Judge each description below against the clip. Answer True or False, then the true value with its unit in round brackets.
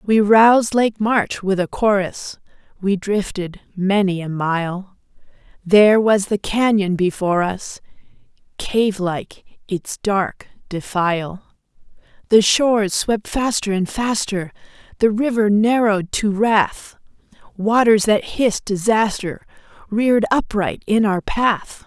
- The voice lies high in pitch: True (205 Hz)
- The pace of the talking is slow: True (115 wpm)